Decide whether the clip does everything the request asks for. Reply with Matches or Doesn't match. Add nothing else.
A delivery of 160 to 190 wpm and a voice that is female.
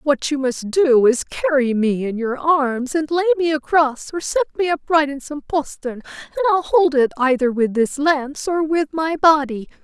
Doesn't match